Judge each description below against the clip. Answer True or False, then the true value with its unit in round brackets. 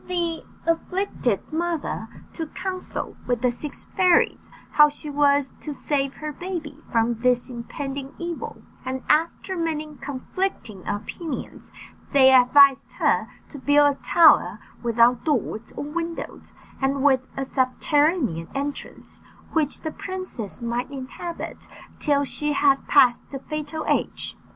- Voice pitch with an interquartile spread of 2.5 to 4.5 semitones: True (3.8 semitones)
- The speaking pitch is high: True (285 Hz)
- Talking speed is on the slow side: True (130 wpm)